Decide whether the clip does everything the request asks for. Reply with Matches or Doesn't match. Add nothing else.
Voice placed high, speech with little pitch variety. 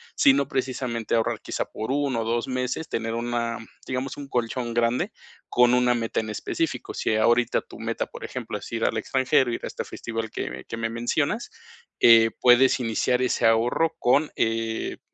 Doesn't match